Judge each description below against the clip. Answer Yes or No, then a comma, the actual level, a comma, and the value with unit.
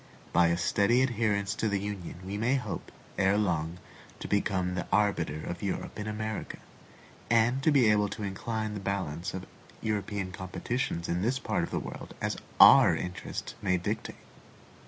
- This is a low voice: Yes, low, 100 Hz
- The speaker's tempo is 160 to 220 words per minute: Yes, average, 165 wpm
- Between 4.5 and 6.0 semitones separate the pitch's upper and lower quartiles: No, average, 3.1 semitones